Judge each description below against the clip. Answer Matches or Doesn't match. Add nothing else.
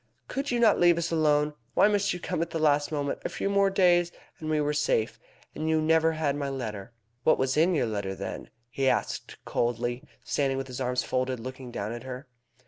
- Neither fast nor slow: Doesn't match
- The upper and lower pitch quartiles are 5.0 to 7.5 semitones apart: Doesn't match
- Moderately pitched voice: Matches